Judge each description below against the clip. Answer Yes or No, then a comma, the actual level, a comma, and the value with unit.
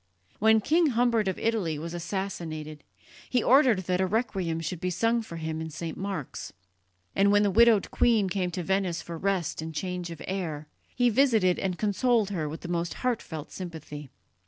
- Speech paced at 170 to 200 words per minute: Yes, average, 180 wpm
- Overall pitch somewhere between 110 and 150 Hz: No, medium, 185 Hz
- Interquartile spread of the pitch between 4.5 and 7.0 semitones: Yes, average, 4.9 semitones